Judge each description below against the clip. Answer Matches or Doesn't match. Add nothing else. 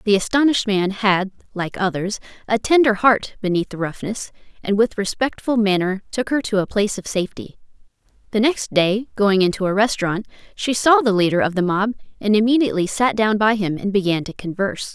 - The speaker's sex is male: Doesn't match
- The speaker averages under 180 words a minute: Doesn't match